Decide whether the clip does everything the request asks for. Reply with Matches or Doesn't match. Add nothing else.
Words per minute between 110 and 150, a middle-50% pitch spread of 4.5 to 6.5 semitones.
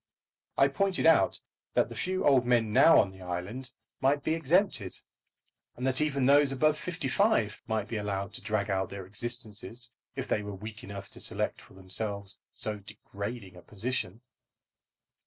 Doesn't match